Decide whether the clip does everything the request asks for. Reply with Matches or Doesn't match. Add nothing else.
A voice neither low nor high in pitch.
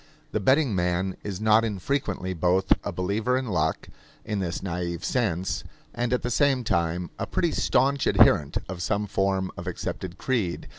Doesn't match